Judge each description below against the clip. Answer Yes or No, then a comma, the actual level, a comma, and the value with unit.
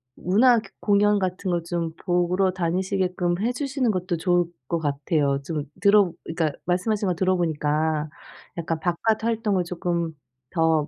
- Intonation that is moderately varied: Yes, average, 3.4 semitones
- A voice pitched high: No, medium, 180 Hz